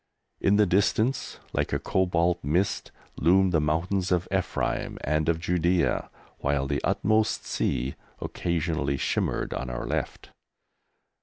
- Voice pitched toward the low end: Yes, very low, 85 Hz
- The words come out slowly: Yes, slow, 130 wpm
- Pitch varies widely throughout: No, average, 3.8 semitones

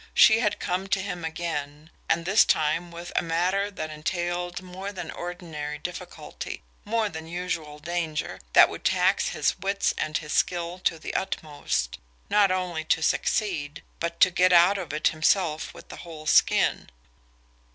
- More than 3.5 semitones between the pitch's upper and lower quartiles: No, average, 2.9 semitones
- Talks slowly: No, average, 160 wpm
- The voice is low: No, medium, 175 Hz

